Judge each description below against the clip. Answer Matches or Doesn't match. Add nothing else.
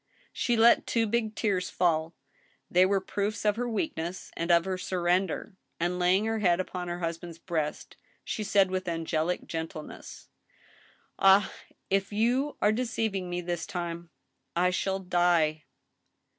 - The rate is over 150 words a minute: Doesn't match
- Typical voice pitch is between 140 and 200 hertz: Matches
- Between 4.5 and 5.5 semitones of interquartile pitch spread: Doesn't match